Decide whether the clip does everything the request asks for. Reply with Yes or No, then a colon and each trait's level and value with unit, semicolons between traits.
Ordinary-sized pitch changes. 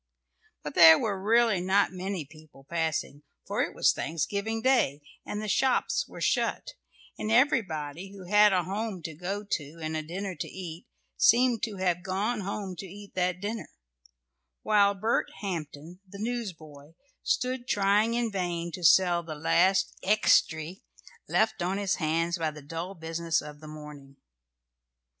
Yes: average, 4.4 semitones